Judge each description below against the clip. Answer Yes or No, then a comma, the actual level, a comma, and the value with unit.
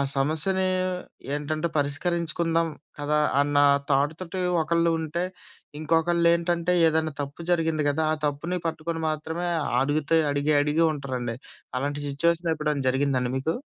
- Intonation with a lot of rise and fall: No, narrow, 2.6 semitones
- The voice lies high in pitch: No, medium, 155 Hz